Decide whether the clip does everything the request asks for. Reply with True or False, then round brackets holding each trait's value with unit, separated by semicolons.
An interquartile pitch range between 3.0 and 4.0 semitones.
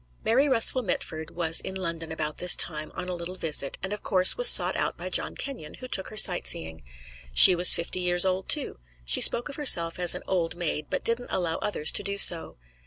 True (3.5 semitones)